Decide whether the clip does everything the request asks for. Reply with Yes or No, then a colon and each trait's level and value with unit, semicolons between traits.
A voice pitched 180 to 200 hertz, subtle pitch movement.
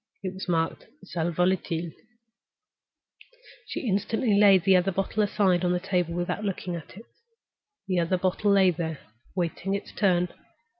Yes: medium, 185 Hz; narrow, 2.1 semitones